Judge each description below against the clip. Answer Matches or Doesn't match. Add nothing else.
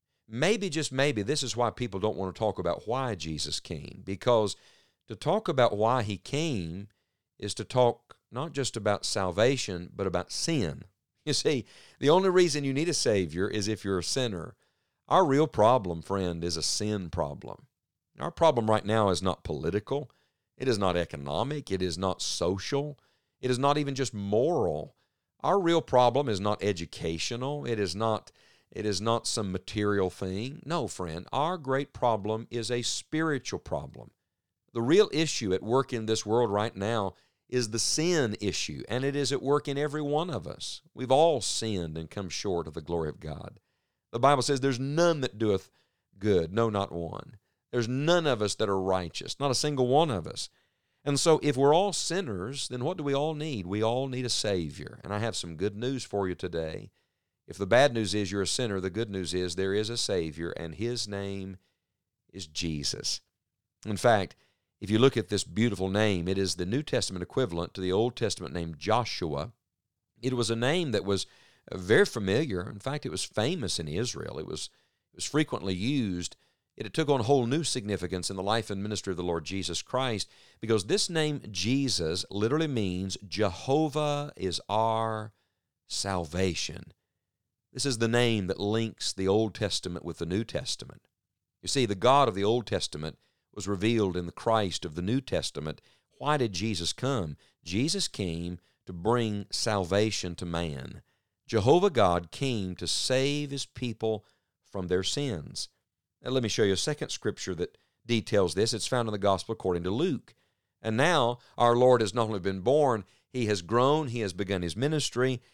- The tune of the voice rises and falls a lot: Matches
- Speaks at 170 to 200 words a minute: Matches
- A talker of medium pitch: Doesn't match